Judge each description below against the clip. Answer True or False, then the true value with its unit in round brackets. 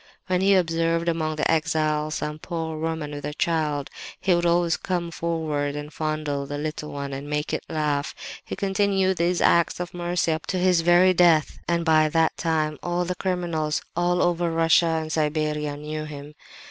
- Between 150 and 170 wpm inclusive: False (185 wpm)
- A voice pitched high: False (160 Hz)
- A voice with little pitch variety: True (2.3 semitones)